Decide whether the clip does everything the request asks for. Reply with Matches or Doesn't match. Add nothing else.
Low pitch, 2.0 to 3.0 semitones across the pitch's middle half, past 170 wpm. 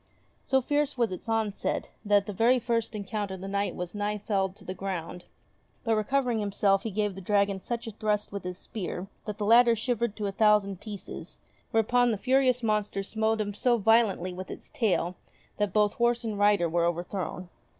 Doesn't match